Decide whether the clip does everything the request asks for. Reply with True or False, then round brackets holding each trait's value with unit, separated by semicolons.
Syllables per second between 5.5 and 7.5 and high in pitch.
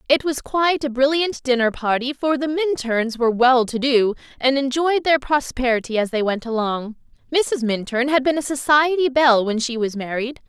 False (5.1 syllables/s; 260 Hz)